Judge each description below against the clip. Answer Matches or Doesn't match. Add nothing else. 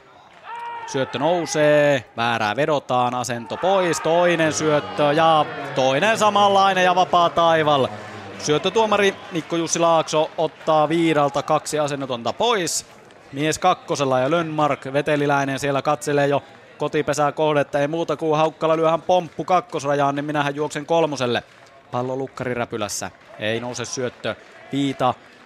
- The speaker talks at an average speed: Matches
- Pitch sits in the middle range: Matches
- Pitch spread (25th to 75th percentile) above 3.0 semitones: Matches